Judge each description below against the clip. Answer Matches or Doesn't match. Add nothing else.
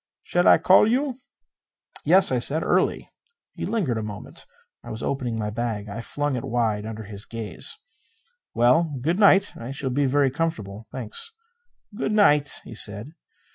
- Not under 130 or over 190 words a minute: Matches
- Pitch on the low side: Matches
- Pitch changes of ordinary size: Doesn't match